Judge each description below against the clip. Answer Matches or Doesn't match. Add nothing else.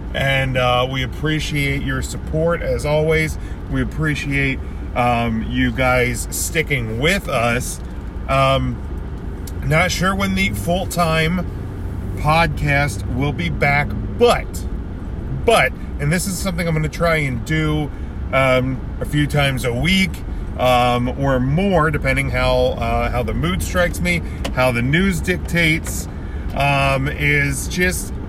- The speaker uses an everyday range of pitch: Doesn't match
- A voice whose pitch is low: Matches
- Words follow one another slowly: Matches